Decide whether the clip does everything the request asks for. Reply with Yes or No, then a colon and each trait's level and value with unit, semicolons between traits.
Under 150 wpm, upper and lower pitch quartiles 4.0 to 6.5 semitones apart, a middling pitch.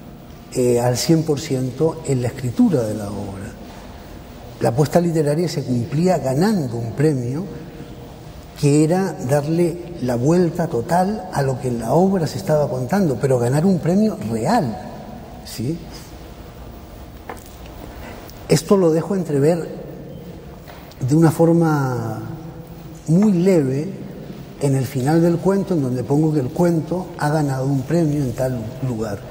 Yes: average, 135 wpm; average, 4.6 semitones; medium, 155 Hz